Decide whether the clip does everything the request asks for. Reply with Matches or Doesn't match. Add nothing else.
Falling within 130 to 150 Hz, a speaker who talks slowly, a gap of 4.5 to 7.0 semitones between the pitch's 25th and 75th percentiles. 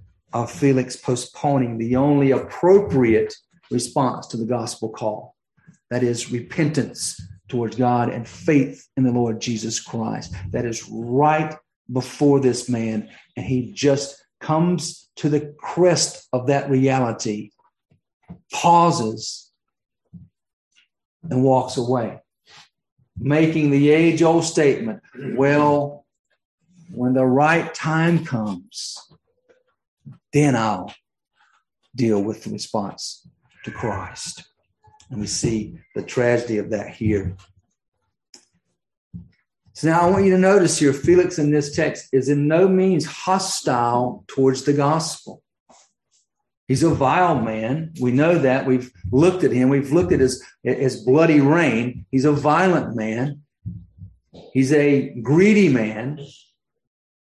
Matches